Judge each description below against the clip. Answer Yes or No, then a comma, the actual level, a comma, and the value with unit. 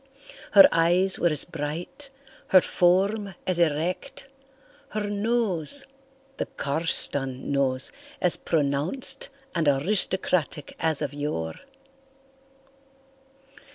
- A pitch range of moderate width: No, wide, 6.5 semitones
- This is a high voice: No, medium, 175 Hz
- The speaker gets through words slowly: Yes, slow, 85 wpm